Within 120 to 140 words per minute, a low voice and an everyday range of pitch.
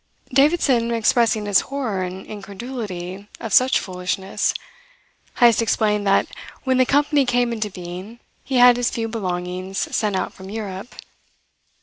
No: slow, 135 wpm; high, 220 Hz; average, 4.3 semitones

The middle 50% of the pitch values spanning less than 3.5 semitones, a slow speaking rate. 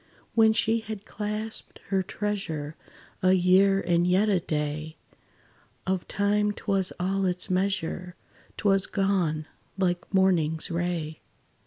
Yes: average, 2.7 semitones; slow, 130 wpm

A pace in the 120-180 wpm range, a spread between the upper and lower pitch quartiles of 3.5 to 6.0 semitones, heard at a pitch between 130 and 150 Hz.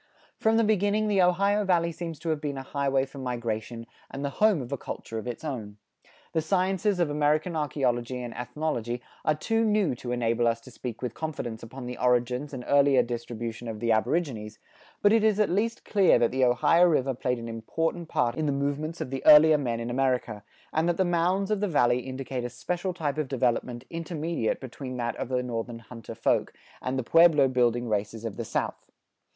No: fast, 205 wpm; wide, 5.6 semitones; low, 135 Hz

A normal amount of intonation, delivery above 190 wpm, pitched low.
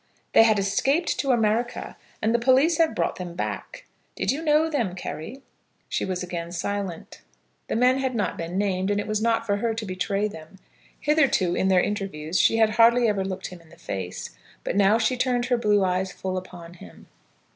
No: average, 4.6 semitones; average, 200 wpm; high, 205 Hz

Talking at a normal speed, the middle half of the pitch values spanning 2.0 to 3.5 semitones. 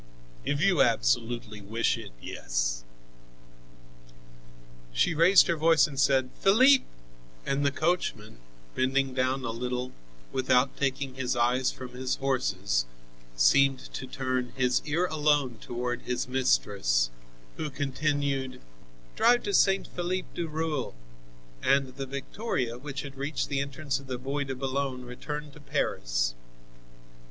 No: slow, 130 wpm; average, 2.8 semitones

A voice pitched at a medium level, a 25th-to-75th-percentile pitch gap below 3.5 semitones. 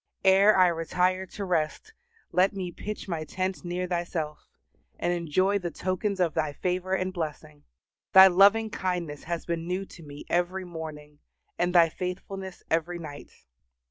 Yes: medium, 180 Hz; narrow, 2.4 semitones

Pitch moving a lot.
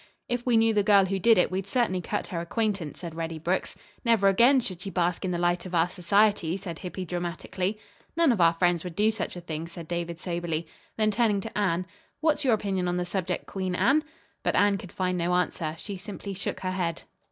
No: average, 3.2 semitones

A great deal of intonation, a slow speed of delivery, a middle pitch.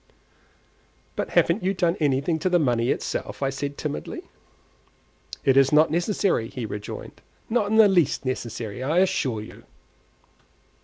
No: wide, 5.9 semitones; average, 145 wpm; medium, 145 Hz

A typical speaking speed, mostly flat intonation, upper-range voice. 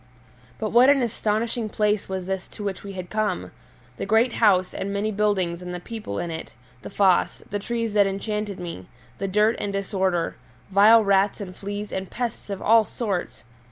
Yes: average, 190 wpm; narrow, 2.3 semitones; high, 200 Hz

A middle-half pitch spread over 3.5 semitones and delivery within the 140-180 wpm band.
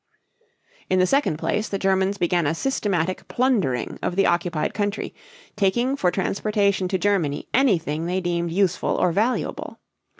No: average, 2.9 semitones; average, 145 wpm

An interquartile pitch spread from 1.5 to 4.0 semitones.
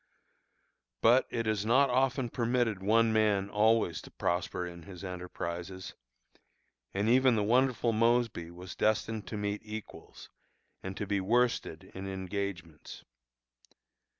Yes: average, 3.7 semitones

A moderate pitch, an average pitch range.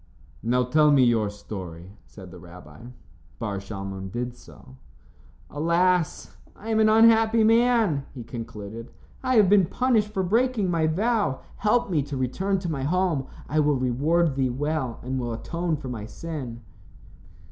No: medium, 145 Hz; wide, 8.3 semitones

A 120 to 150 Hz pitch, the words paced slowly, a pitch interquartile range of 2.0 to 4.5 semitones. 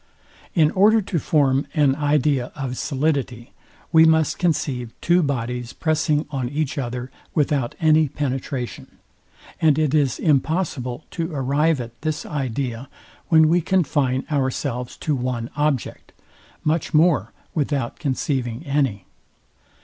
Yes: medium, 140 Hz; slow, 125 wpm; average, 3.6 semitones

